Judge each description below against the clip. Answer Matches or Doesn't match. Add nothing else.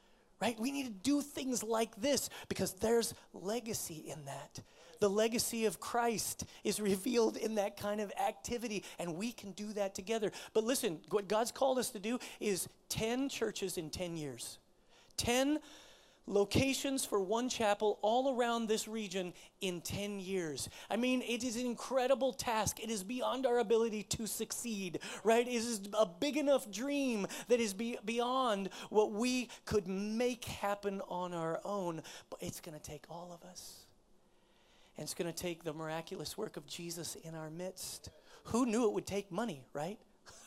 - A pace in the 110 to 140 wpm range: Doesn't match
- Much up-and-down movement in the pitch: Doesn't match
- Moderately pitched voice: Doesn't match